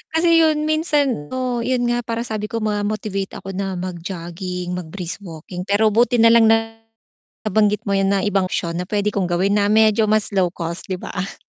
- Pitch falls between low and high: No, high, 205 Hz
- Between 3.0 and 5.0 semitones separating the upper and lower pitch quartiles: Yes, average, 3.4 semitones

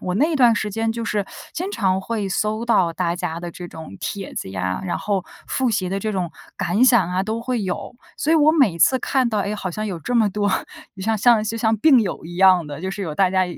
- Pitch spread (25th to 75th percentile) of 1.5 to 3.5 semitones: No, average, 4.1 semitones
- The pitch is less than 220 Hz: Yes, high, 205 Hz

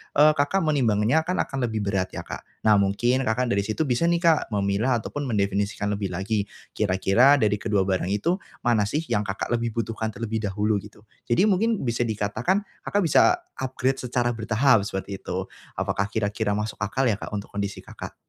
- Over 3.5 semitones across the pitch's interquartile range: Yes, average, 4.4 semitones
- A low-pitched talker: Yes, low, 110 Hz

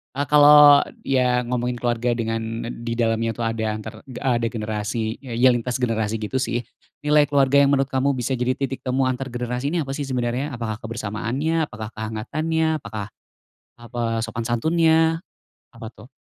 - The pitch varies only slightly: No, average, 3.3 semitones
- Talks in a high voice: No, low, 125 Hz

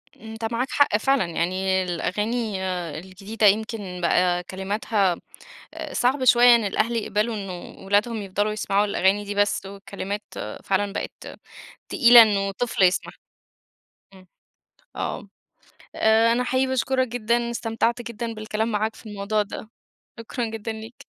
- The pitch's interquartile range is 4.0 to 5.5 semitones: No, average, 2.9 semitones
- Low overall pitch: No, high, 215 Hz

